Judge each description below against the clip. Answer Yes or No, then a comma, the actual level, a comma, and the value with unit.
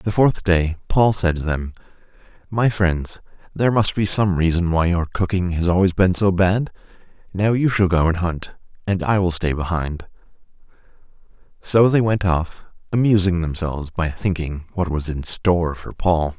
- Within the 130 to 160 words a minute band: No, average, 170 wpm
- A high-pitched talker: No, very low, 90 Hz